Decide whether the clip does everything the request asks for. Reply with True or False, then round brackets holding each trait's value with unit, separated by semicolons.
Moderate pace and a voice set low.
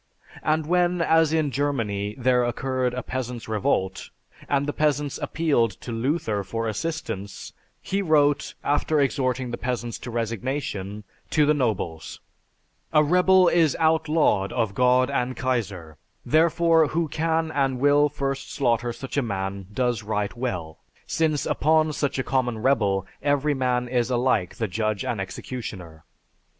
True (145 wpm; 130 Hz)